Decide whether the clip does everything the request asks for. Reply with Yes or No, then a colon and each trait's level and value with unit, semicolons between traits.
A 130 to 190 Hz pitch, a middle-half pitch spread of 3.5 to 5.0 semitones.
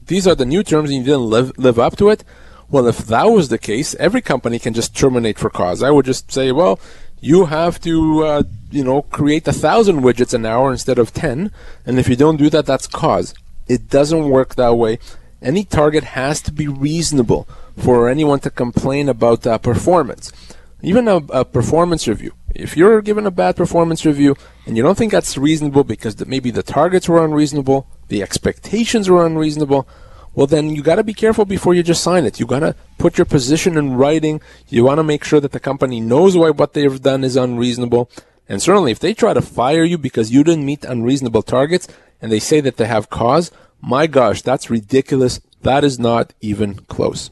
Yes: medium, 140 Hz; average, 4.4 semitones